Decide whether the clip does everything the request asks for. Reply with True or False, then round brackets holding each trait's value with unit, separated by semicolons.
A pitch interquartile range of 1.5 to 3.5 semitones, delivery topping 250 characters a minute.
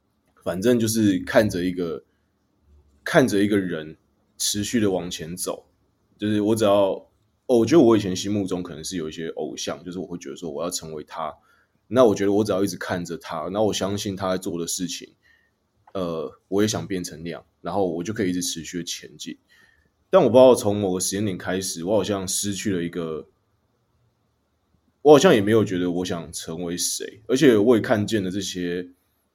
True (2.8 semitones; 285 characters per minute)